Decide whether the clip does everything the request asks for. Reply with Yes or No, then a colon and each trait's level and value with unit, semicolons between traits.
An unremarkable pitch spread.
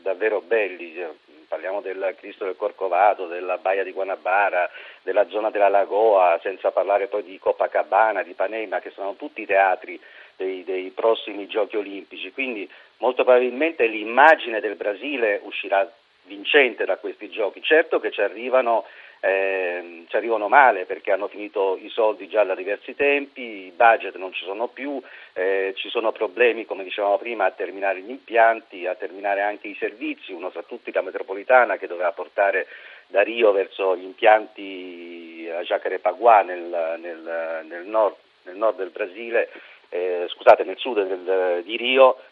No: wide, 6.1 semitones